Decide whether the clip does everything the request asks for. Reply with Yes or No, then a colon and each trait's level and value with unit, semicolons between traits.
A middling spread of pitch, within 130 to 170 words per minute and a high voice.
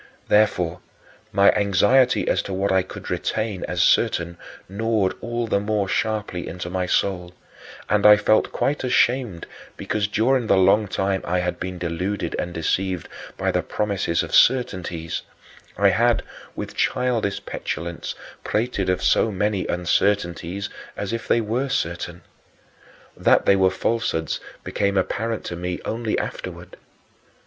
No: average, 3.5 semitones; average, 145 wpm; low, 100 Hz